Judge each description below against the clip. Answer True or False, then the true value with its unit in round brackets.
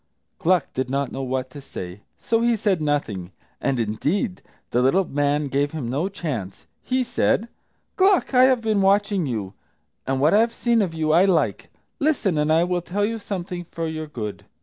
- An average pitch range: False (7.1 semitones)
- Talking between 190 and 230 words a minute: True (195 wpm)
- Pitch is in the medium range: True (160 Hz)